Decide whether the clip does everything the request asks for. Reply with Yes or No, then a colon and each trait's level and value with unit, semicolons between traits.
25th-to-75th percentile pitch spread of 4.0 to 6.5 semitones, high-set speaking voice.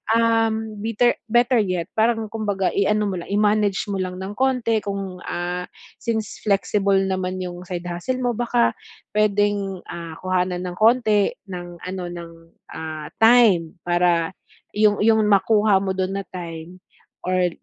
No: average, 3.3 semitones; high, 200 Hz